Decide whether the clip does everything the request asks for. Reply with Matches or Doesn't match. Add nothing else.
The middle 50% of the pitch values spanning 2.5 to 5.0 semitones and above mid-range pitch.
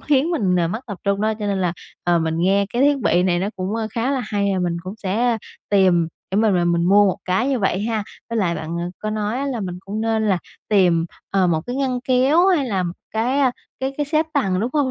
Doesn't match